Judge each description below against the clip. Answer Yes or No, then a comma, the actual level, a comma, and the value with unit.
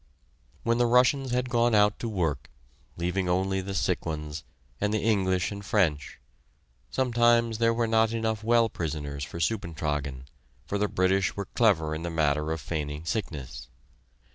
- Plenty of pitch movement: Yes, wide, 6.2 semitones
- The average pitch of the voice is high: No, very low, 95 Hz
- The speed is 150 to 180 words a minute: Yes, average, 160 wpm